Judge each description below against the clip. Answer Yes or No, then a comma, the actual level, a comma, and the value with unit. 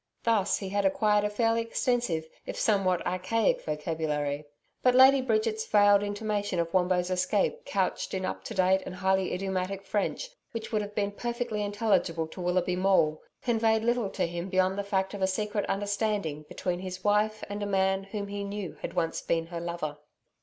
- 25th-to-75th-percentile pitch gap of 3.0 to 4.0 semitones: No, narrow, 2.6 semitones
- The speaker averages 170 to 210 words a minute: Yes, average, 180 wpm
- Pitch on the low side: No, high, 195 Hz